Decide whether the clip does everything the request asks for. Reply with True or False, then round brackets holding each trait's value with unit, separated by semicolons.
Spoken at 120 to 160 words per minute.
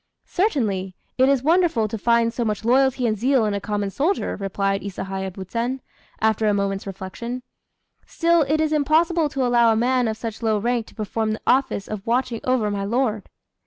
False (190 wpm)